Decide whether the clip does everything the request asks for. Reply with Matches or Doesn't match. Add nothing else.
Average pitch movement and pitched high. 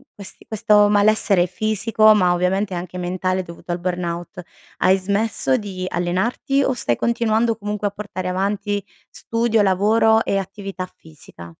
Matches